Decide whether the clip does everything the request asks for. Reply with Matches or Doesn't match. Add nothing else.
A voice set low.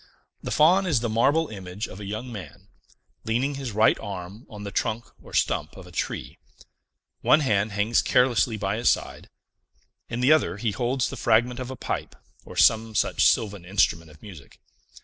Matches